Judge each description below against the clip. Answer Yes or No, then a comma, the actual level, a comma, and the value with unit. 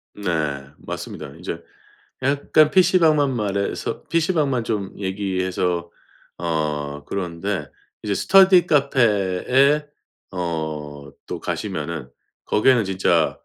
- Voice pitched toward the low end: Yes, low, 100 Hz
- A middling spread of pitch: No, wide, 8.3 semitones